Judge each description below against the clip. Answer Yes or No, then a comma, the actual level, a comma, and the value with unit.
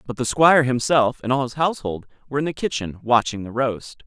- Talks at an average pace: No, fast, 220 wpm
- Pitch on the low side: Yes, low, 130 Hz